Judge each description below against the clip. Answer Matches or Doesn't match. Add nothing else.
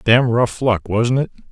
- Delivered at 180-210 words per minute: Matches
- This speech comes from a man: Matches